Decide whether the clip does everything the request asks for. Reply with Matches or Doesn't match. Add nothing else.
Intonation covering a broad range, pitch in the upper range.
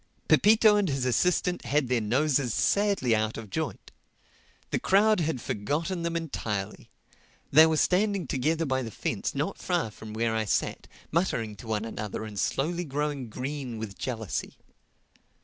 Doesn't match